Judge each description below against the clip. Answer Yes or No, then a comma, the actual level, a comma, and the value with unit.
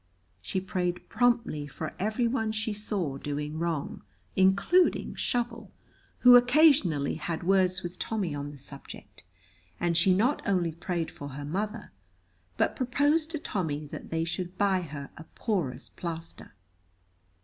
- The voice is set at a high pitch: No, medium, 180 Hz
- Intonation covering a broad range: Yes, wide, 5.9 semitones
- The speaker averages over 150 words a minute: No, average, 140 wpm